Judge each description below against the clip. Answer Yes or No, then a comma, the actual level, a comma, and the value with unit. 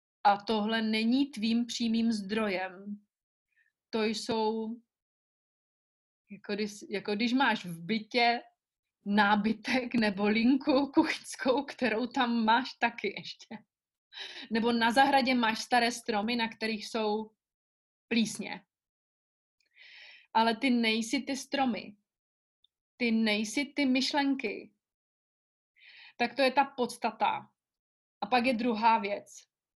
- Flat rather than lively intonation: No, average, 3.2 semitones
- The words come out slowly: Yes, slow, 105 wpm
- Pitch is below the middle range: No, high, 230 Hz